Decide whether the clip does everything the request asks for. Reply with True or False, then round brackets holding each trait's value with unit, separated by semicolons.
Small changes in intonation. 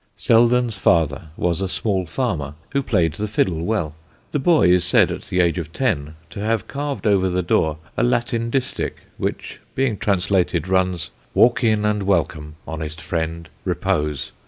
False (5.6 semitones)